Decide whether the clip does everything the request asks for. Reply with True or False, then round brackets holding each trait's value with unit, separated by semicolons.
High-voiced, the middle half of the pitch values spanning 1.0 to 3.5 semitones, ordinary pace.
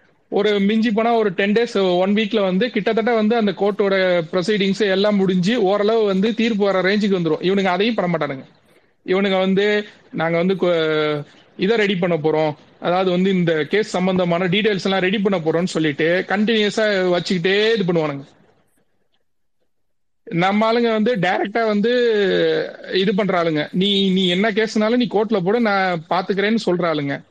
False (195 Hz; 3.1 semitones; 145 wpm)